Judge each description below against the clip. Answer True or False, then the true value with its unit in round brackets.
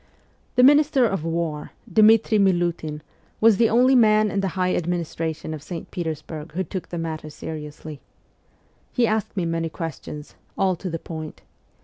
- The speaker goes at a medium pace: True (160 wpm)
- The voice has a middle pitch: True (175 Hz)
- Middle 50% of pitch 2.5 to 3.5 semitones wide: False (5.1 semitones)